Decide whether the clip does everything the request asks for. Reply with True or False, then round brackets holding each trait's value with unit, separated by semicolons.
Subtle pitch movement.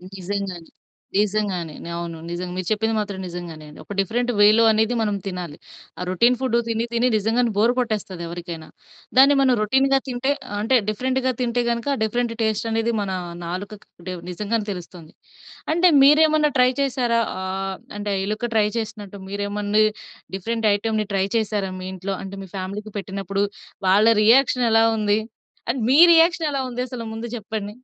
False (3.7 semitones)